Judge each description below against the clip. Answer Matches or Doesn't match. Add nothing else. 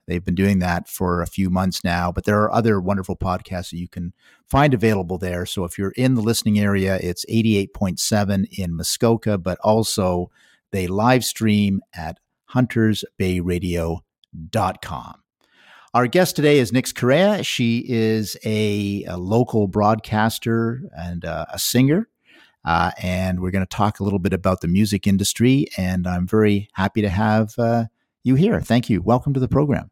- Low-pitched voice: Matches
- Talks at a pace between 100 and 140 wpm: Doesn't match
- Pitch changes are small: Doesn't match